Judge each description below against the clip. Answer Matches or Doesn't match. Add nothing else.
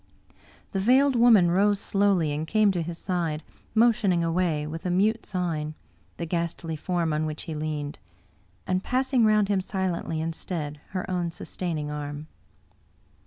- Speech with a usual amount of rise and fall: Matches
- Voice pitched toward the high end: Doesn't match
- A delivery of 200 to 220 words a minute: Doesn't match